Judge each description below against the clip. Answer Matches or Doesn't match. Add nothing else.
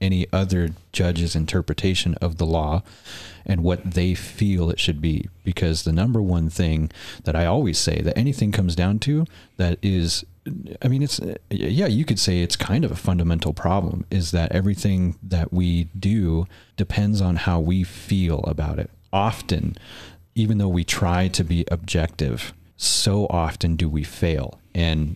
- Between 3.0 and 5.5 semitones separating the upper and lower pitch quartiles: Doesn't match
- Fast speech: Doesn't match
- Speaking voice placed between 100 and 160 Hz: Doesn't match